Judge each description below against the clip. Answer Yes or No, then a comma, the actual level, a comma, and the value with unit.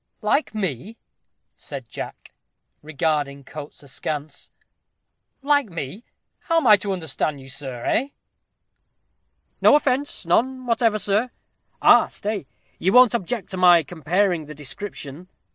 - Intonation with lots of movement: Yes, wide, 7.4 semitones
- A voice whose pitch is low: No, medium, 185 Hz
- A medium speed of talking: No, slow, 125 wpm